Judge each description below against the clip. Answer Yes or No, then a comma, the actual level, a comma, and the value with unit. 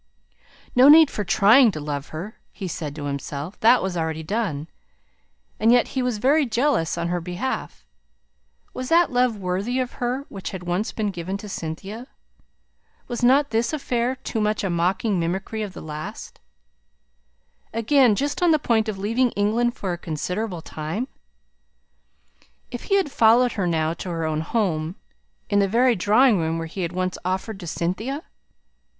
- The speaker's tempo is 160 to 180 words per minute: Yes, average, 170 wpm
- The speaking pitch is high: Yes, high, 205 Hz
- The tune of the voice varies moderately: No, wide, 6.0 semitones